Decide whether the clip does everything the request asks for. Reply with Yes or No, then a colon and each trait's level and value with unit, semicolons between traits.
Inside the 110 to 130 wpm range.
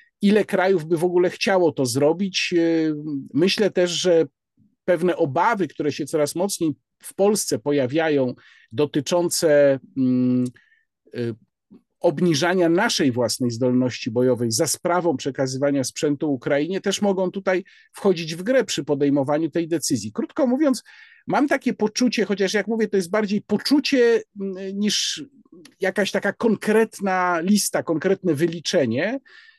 Yes: average, 120 wpm